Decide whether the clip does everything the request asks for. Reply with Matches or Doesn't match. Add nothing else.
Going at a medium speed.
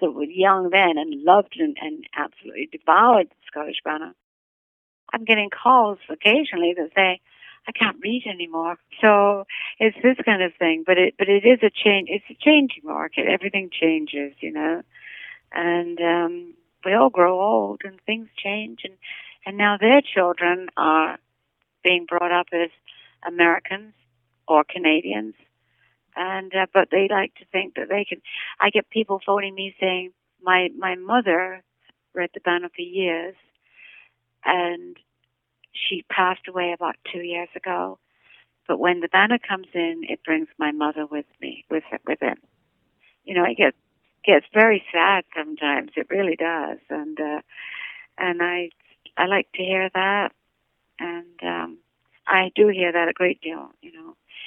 Matches